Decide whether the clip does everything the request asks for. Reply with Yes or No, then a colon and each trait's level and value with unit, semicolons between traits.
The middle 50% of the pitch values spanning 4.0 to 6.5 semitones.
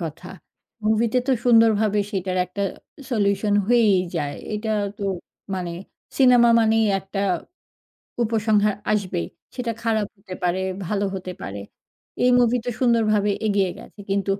No: average, 2.8 semitones